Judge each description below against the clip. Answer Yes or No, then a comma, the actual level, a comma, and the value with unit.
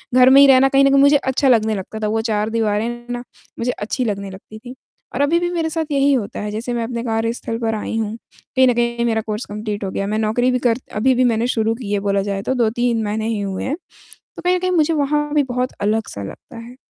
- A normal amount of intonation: Yes, average, 3.4 semitones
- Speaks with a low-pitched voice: No, high, 235 Hz